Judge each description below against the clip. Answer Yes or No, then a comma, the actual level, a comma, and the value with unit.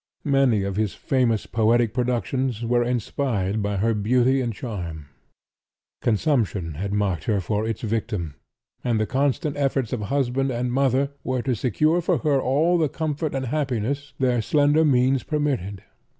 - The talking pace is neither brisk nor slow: Yes, average, 155 wpm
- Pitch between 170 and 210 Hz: No, low, 125 Hz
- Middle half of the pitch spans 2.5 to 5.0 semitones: Yes, average, 4.3 semitones